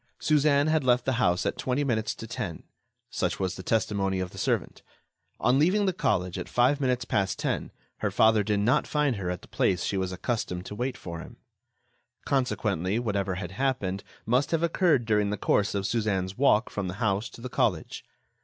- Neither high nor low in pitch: No, low, 110 Hz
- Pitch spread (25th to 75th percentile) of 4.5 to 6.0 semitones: Yes, wide, 5.4 semitones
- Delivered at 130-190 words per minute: No, average, 200 wpm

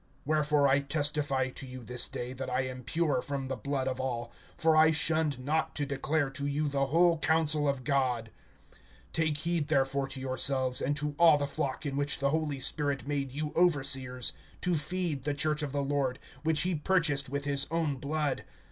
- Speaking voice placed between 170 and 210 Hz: No, medium, 140 Hz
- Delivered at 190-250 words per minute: Yes, average, 195 wpm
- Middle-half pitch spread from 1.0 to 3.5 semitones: Yes, narrow, 2.5 semitones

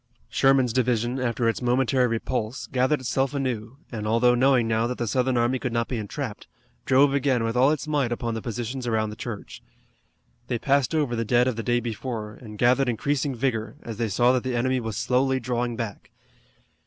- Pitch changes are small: Yes, narrow, 2.3 semitones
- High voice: No, low, 120 Hz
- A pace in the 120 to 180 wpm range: No, average, 200 wpm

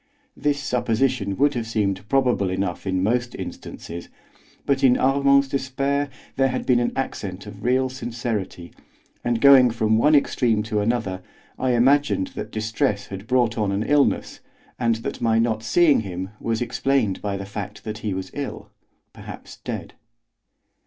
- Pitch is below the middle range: Yes, low, 115 Hz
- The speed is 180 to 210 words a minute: No, average, 160 wpm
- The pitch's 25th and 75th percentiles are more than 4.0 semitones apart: Yes, average, 4.4 semitones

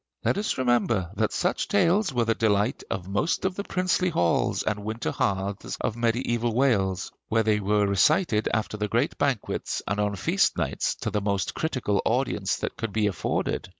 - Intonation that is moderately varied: Yes, average, 4.1 semitones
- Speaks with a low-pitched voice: Yes, low, 110 Hz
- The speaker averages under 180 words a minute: No, average, 185 wpm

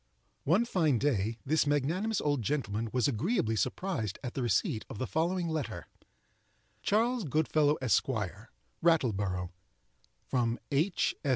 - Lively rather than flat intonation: Yes, wide, 6.5 semitones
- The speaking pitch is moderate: Yes, medium, 145 Hz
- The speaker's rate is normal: No, slow, 120 wpm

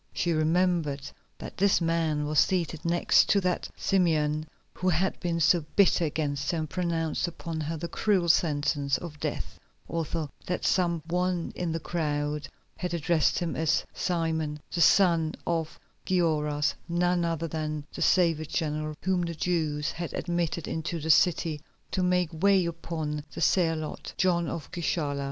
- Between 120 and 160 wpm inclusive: Yes, average, 155 wpm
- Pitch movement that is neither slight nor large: No, narrow, 2.3 semitones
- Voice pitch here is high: No, medium, 165 Hz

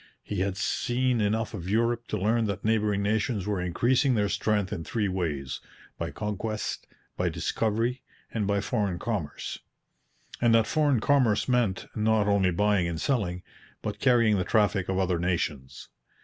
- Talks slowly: No, average, 160 wpm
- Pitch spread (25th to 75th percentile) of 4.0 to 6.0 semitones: No, average, 3.5 semitones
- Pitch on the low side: Yes, low, 105 Hz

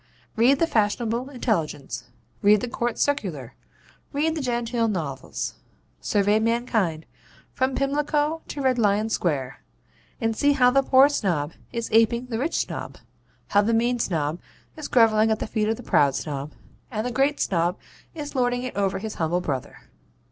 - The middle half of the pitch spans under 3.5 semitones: No, average, 5.1 semitones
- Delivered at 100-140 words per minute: No, average, 160 wpm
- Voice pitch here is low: No, high, 225 Hz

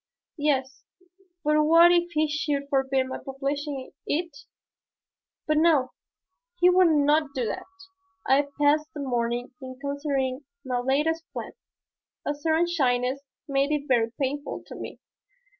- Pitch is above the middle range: Yes, very high, 285 Hz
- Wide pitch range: No, narrow, 2.5 semitones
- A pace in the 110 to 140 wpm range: Yes, slow, 135 wpm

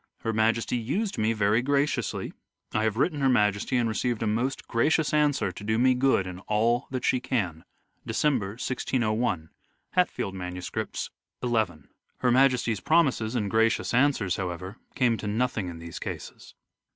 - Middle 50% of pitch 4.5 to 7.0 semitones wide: No, average, 3.8 semitones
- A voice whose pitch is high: No, low, 115 Hz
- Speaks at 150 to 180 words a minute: Yes, average, 155 wpm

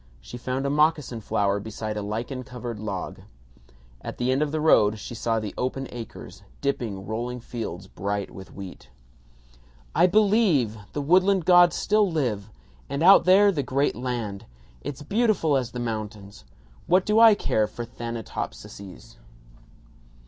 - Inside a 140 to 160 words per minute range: Yes, average, 150 wpm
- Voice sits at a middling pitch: No, low, 125 Hz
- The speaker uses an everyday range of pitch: No, wide, 6.6 semitones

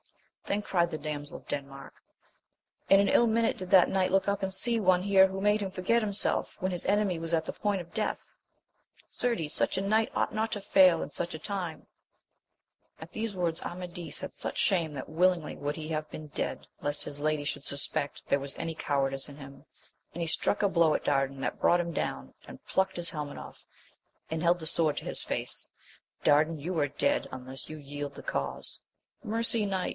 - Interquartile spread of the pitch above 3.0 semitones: Yes, average, 4.7 semitones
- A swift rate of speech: Yes, fast, 210 wpm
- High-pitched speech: No, medium, 170 Hz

